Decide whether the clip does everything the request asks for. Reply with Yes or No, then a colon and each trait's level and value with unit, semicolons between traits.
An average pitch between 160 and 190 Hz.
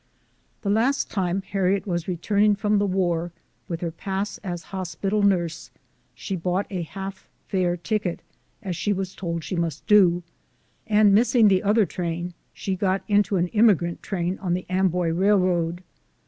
Yes: medium, 185 Hz